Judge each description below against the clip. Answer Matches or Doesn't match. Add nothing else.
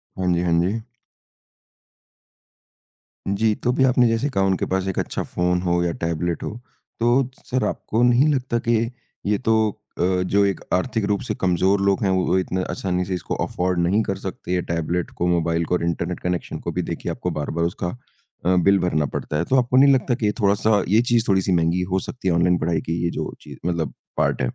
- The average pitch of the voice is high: Doesn't match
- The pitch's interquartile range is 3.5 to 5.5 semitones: Matches